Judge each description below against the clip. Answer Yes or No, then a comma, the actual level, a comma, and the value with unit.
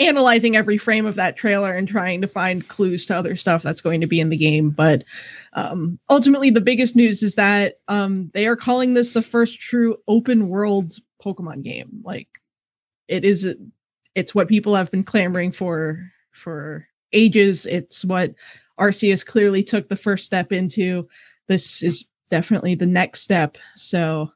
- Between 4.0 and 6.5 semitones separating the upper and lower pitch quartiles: No, average, 3.4 semitones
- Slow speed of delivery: No, average, 170 wpm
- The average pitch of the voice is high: Yes, high, 195 Hz